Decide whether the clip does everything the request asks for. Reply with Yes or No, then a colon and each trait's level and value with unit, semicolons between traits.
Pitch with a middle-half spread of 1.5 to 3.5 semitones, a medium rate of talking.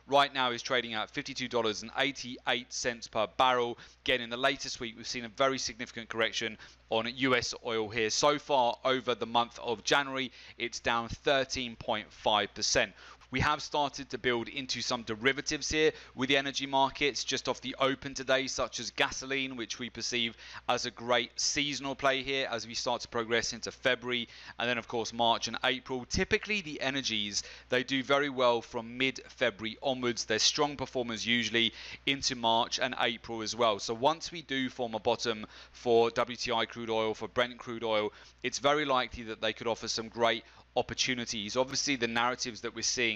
Yes: narrow, 2.5 semitones; average, 180 wpm